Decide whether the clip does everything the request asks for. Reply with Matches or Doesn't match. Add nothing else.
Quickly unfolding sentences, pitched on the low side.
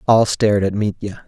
Doesn't match